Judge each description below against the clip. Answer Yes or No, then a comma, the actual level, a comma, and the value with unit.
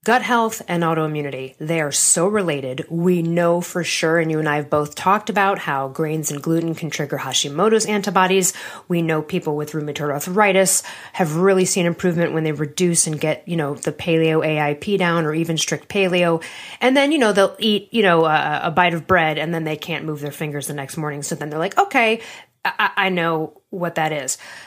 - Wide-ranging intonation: No, average, 3.5 semitones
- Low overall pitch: No, medium, 165 Hz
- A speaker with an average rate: No, fast, 210 wpm